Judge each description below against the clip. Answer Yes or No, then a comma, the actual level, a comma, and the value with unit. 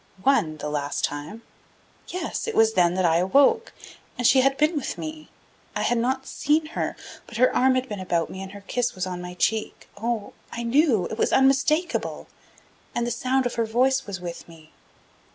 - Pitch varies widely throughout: Yes, wide, 6.4 semitones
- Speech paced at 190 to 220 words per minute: Yes, average, 200 wpm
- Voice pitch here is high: Yes, high, 235 Hz